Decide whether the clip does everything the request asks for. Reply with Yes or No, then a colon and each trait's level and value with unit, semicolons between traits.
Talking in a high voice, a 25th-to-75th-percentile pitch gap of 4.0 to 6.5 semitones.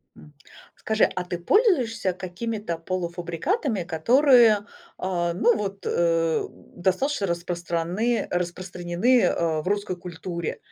No: medium, 180 Hz; average, 4.4 semitones